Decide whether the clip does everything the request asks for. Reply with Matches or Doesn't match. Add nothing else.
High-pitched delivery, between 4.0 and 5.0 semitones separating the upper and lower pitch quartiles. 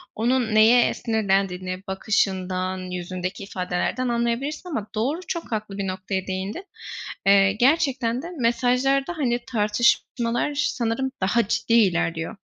Matches